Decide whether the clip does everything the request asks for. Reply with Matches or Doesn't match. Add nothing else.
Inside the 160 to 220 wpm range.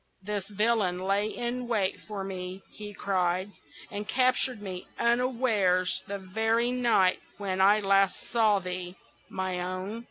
Doesn't match